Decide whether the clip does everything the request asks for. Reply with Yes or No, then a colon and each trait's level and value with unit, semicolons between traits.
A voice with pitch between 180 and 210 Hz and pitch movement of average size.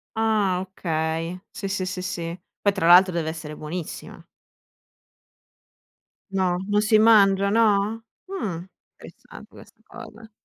Yes: high, 190 Hz; average, 3.5 semitones